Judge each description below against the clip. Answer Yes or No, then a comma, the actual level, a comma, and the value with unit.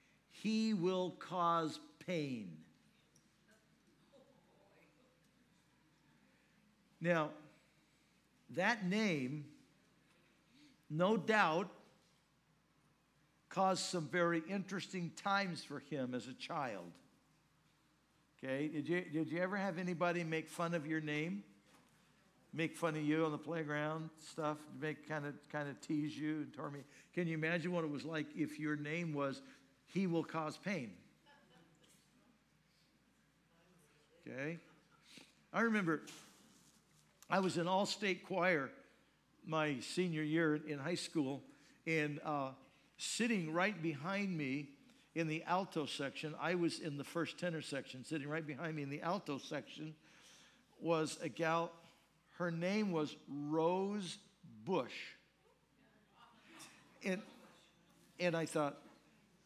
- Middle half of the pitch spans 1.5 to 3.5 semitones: Yes, average, 2.9 semitones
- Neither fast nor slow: No, slow, 115 wpm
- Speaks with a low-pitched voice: No, medium, 165 Hz